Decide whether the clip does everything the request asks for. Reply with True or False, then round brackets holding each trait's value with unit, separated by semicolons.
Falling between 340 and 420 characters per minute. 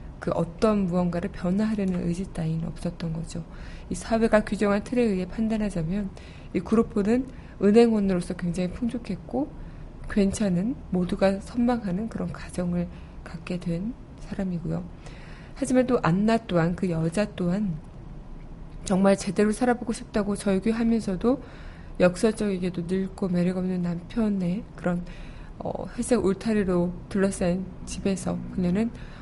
False (295 characters per minute)